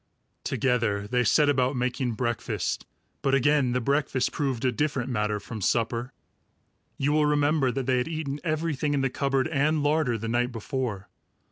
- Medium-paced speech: Yes, average, 165 wpm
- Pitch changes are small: No, average, 3.2 semitones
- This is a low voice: Yes, low, 130 Hz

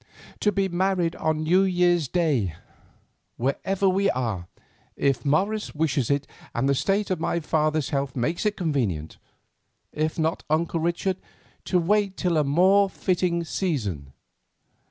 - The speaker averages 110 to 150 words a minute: Yes, average, 140 wpm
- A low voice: No, medium, 165 Hz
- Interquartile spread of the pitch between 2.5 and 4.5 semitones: No, average, 5.0 semitones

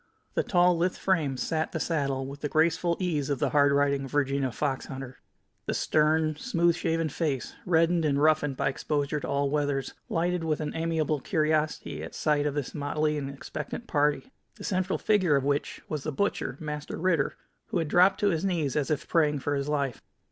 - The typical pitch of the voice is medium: Yes, medium, 150 Hz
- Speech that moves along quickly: No, average, 195 wpm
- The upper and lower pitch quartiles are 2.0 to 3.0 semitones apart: Yes, average, 2.7 semitones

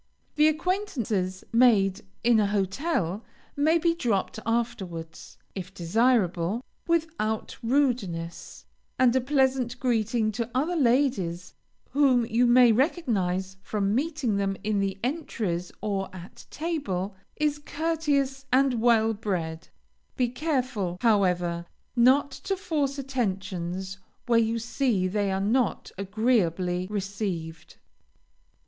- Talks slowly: Yes, slow, 115 wpm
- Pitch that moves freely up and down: Yes, wide, 5.7 semitones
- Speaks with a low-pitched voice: No, high, 225 Hz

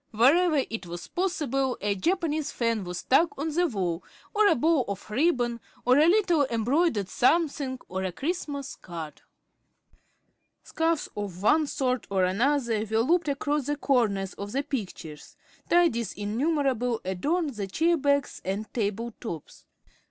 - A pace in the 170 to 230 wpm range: No, average, 145 wpm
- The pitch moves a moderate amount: No, wide, 6.8 semitones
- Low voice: No, very high, 255 Hz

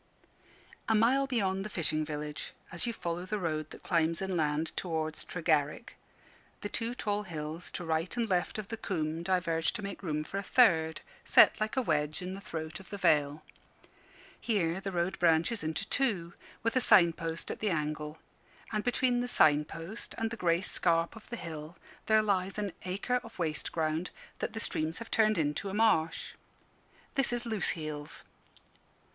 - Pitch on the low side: No, medium, 175 Hz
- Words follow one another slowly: No, average, 180 wpm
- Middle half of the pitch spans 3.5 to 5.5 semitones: Yes, average, 5.1 semitones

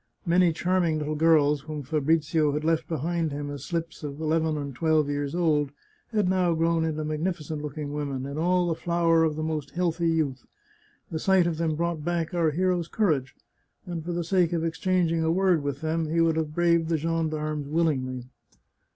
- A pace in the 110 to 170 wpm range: No, average, 190 wpm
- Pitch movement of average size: No, narrow, 2.1 semitones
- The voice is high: No, medium, 160 Hz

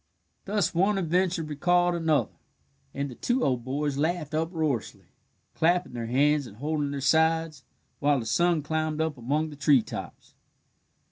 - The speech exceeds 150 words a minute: No, average, 145 wpm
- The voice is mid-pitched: Yes, medium, 155 Hz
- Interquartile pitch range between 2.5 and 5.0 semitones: Yes, average, 3.1 semitones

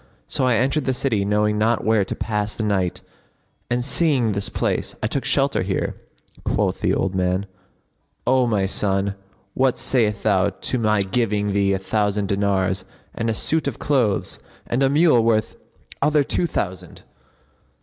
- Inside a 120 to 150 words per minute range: No, average, 165 wpm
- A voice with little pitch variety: No, average, 4.0 semitones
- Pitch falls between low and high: No, low, 105 Hz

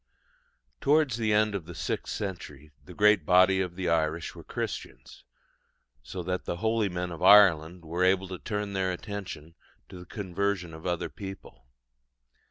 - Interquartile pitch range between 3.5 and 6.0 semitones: No, average, 3.0 semitones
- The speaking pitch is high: No, very low, 90 Hz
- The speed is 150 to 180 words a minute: Yes, average, 165 wpm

